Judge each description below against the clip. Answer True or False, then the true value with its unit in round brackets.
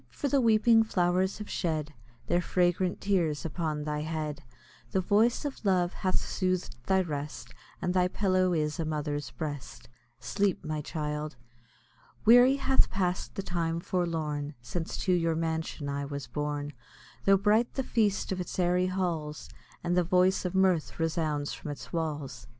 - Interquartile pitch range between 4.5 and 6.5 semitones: False (3.9 semitones)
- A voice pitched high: False (175 Hz)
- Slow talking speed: False (160 wpm)